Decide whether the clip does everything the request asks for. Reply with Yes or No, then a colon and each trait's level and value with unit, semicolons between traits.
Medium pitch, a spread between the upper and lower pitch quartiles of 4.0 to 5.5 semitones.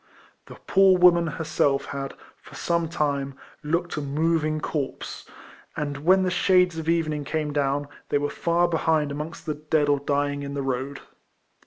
No: medium, 150 Hz; average, 2.8 semitones